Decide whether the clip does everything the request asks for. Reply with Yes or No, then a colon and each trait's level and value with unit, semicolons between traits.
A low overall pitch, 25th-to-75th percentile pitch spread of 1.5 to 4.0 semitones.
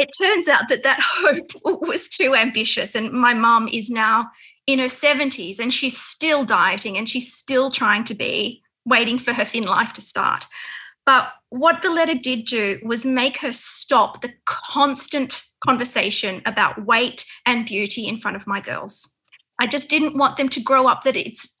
No: very high, 250 Hz; average, 3.6 semitones